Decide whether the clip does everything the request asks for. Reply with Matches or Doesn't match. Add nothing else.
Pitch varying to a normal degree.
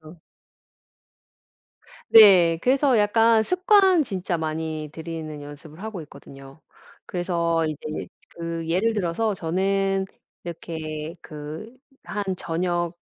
Matches